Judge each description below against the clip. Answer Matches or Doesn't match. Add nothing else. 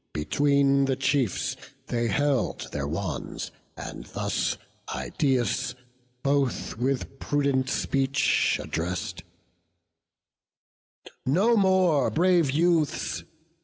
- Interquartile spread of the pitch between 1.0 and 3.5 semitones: Matches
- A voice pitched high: Doesn't match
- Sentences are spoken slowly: Matches